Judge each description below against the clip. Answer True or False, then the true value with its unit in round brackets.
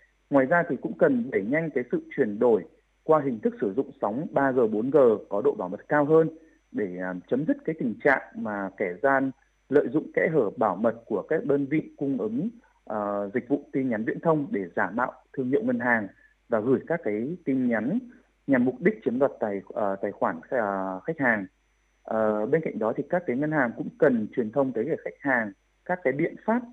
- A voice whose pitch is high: False (150 Hz)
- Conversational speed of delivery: True (220 wpm)